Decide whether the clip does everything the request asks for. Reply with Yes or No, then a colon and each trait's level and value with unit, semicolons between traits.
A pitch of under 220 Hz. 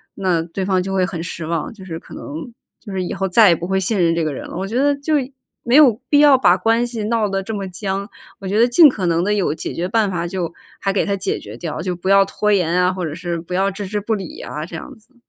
Yes: high, 190 Hz